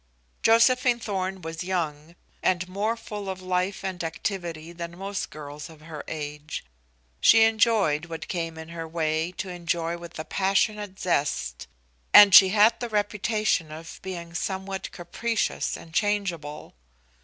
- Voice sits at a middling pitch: Yes, medium, 180 Hz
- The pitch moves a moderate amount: Yes, average, 4.0 semitones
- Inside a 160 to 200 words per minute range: No, average, 145 wpm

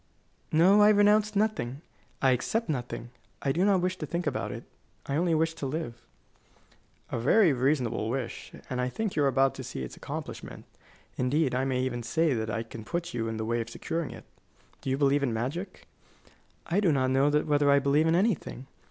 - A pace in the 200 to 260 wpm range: Yes, fast, 205 wpm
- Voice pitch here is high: No, medium, 140 Hz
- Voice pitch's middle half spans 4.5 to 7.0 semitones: Yes, average, 5.3 semitones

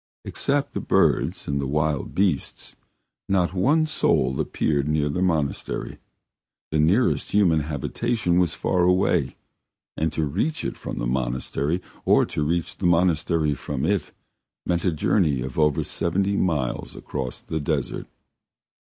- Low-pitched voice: Yes, very low, 80 Hz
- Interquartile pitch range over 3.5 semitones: Yes, average, 4.2 semitones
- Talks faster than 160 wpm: No, average, 140 wpm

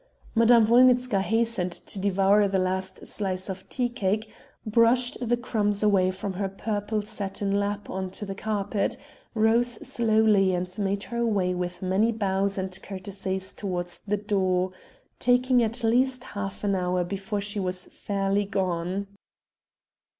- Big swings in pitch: No, average, 2.7 semitones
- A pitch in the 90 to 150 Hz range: No, high, 200 Hz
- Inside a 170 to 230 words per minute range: No, average, 145 wpm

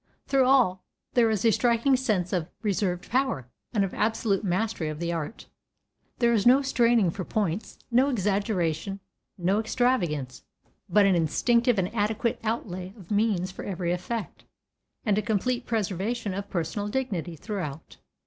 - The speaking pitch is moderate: No, high, 205 Hz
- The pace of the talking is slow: No, average, 150 wpm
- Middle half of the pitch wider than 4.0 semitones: Yes, average, 4.5 semitones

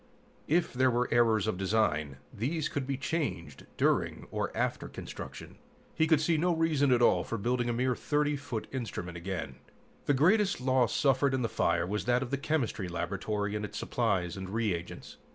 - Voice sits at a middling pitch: No, low, 120 Hz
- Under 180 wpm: No, average, 185 wpm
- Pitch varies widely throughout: Yes, wide, 5.8 semitones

